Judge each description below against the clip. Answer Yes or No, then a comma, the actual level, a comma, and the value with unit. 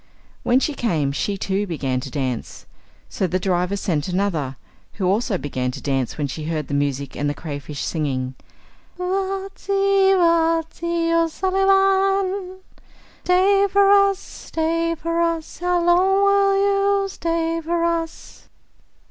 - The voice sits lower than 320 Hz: No, very high, 330 Hz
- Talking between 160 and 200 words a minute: No, average, 145 wpm